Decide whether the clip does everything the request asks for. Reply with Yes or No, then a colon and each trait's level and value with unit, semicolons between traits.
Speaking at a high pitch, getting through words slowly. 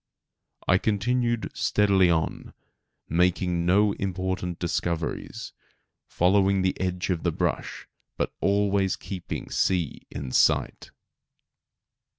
No: very low, 95 Hz; slow, 105 wpm